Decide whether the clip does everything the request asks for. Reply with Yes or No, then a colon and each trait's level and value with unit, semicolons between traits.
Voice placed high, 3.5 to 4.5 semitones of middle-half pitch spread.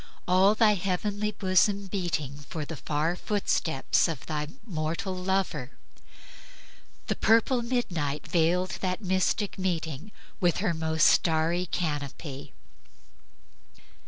No: medium, 180 Hz; average, 3.8 semitones